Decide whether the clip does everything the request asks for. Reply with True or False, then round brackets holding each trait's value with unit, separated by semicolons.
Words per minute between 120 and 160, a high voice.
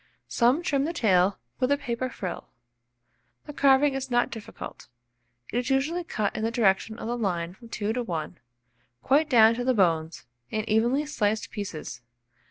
False (175 wpm; 235 Hz)